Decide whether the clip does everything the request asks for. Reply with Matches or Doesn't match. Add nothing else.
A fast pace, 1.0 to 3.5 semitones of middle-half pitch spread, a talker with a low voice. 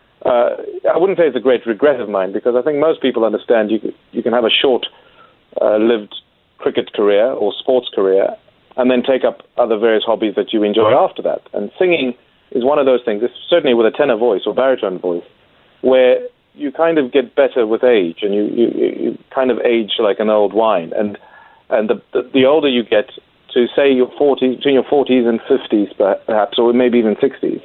Doesn't match